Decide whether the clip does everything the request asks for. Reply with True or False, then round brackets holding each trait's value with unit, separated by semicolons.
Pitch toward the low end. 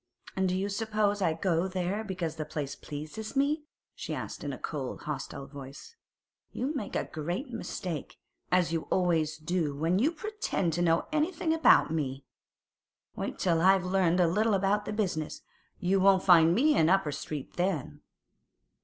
False (180 Hz)